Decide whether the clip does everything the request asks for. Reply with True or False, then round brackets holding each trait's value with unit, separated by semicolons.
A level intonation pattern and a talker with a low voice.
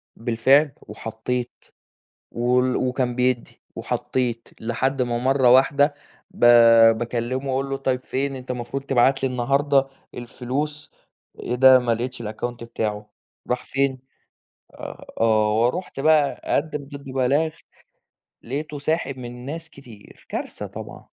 True (2.3 semitones; 130 Hz)